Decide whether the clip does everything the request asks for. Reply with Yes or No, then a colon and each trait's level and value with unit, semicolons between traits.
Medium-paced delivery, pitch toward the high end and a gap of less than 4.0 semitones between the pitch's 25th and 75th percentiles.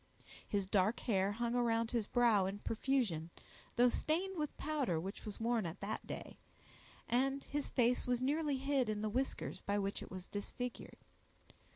No: average, 170 wpm; high, 235 Hz; average, 4.5 semitones